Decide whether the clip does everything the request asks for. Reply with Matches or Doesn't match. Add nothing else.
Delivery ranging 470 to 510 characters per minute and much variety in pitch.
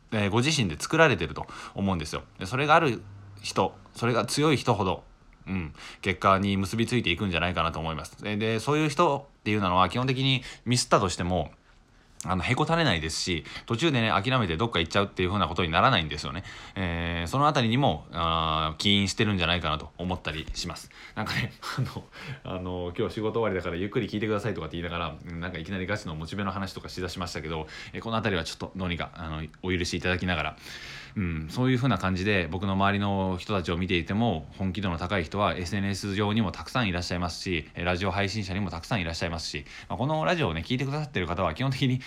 Doesn't match